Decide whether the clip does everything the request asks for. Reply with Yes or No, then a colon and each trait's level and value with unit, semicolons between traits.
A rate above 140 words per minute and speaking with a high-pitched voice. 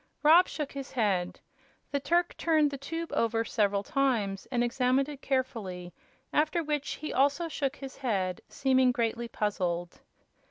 Yes: average, 150 wpm; very high, 260 Hz